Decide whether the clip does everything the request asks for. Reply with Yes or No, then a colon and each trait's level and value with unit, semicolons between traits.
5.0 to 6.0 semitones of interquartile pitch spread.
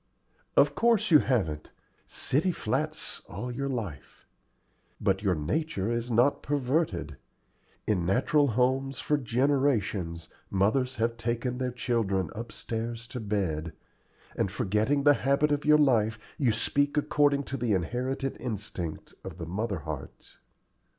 Yes: wide, 5.5 semitones